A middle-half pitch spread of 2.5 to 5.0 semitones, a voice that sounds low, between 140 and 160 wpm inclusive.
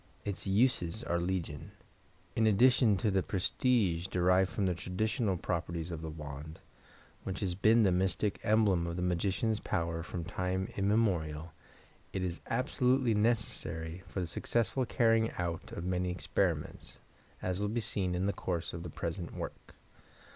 Yes: average, 4.1 semitones; very low, 95 Hz; average, 155 wpm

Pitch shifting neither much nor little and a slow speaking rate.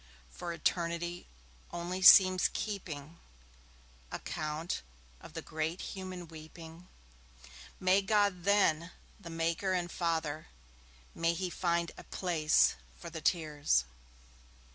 No: narrow, 2.2 semitones; slow, 105 wpm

